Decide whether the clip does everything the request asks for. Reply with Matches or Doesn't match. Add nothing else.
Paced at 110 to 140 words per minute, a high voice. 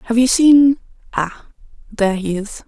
Matches